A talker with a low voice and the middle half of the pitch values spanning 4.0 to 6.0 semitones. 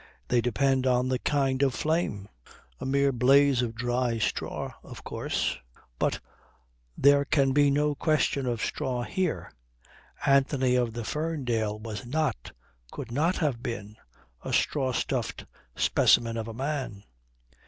No: low, 130 Hz; average, 3.2 semitones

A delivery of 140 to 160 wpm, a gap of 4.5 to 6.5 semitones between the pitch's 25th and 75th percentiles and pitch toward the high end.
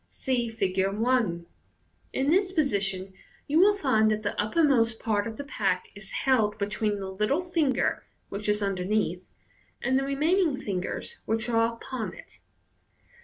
Yes: average, 155 wpm; average, 5.1 semitones; high, 225 Hz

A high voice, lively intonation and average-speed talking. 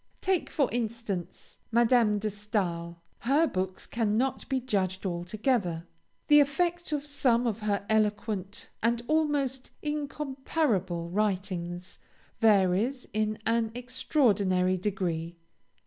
No: high, 215 Hz; wide, 5.7 semitones; slow, 105 wpm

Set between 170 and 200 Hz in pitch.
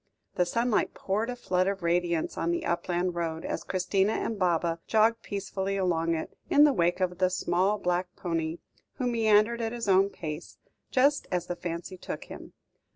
Yes: medium, 185 Hz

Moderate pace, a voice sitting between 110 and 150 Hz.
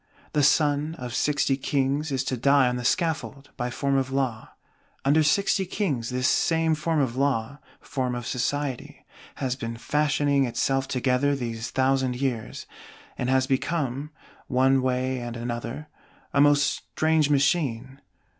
Yes: average, 145 wpm; low, 135 Hz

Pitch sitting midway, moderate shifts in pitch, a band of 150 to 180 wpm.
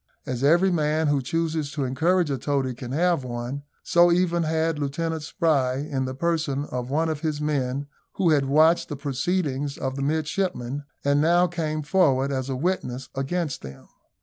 Yes: medium, 145 Hz; average, 3.5 semitones; average, 175 wpm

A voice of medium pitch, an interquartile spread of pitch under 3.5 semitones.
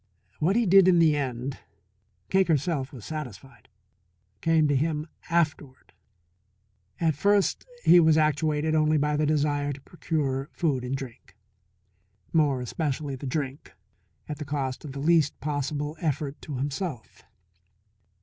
Yes: medium, 150 Hz; average, 2.7 semitones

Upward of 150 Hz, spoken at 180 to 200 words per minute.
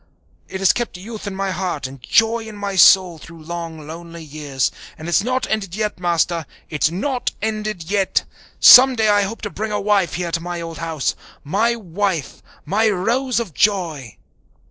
Yes: high, 190 Hz; average, 185 wpm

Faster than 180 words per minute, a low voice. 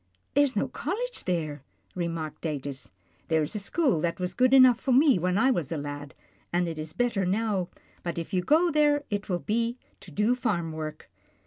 No: fast, 205 wpm; medium, 185 Hz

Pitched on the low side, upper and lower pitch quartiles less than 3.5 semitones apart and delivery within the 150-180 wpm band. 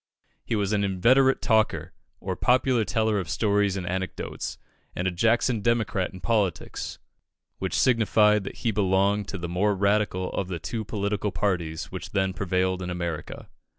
Yes: low, 100 Hz; average, 2.7 semitones; average, 160 wpm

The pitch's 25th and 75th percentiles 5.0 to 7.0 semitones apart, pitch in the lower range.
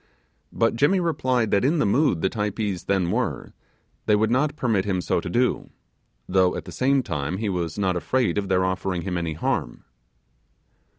Yes: wide, 5.4 semitones; low, 100 Hz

